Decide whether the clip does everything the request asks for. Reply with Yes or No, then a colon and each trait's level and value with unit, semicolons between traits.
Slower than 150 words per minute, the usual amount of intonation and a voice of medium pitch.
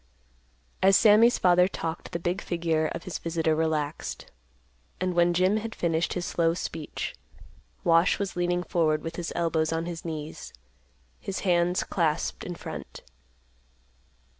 No: average, 140 wpm; narrow, 1.7 semitones; medium, 170 Hz